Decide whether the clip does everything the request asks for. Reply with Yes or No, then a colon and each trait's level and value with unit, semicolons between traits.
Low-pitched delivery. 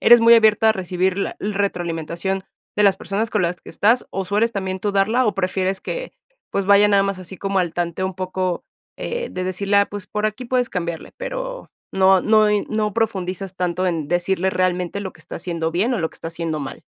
No: high, 195 Hz